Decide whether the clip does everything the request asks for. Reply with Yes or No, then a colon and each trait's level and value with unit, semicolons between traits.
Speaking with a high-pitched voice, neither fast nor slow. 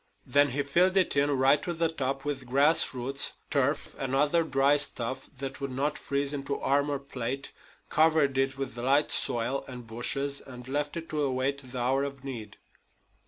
No: medium, 140 Hz; average, 185 wpm